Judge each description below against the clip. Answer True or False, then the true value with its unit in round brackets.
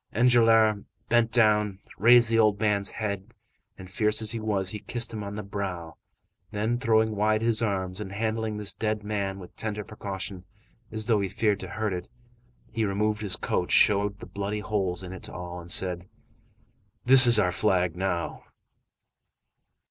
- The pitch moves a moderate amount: False (2.3 semitones)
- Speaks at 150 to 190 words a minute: True (175 wpm)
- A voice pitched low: True (105 Hz)